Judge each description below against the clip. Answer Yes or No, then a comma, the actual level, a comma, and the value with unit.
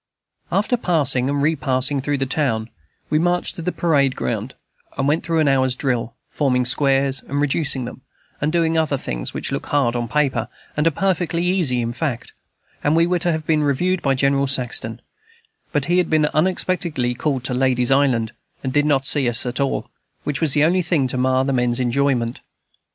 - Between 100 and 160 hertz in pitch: Yes, medium, 140 Hz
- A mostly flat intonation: No, average, 3.6 semitones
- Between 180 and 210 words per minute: Yes, average, 195 wpm